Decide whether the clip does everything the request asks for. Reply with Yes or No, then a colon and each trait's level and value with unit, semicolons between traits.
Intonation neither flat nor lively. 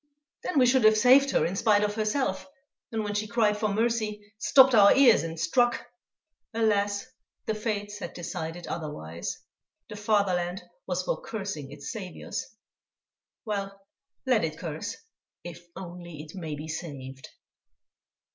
Yes: average, 4.5 semitones